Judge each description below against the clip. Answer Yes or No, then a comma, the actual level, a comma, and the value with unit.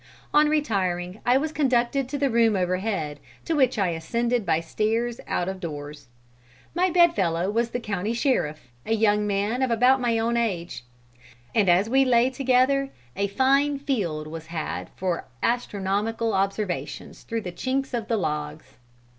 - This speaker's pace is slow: No, average, 165 wpm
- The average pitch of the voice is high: Yes, high, 225 Hz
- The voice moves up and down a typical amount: No, wide, 5.8 semitones